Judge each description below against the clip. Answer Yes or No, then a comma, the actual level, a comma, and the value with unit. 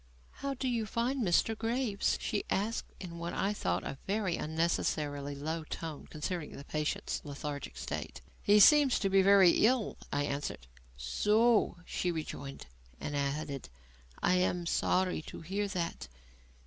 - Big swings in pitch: Yes, wide, 6.0 semitones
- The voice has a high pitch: No, medium, 175 Hz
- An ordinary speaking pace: Yes, average, 150 wpm